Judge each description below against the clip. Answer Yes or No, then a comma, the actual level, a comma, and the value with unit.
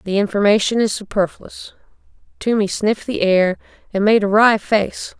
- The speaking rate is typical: Yes, average, 150 wpm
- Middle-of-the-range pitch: No, high, 205 Hz